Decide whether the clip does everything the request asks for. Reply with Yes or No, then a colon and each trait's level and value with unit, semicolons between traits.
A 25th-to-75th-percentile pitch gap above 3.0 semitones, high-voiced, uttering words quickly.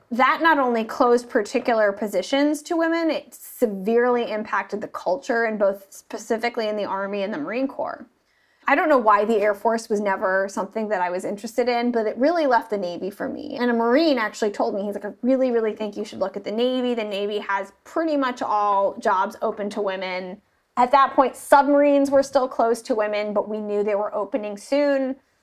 Yes: average, 4.7 semitones; high, 230 Hz; fast, 210 wpm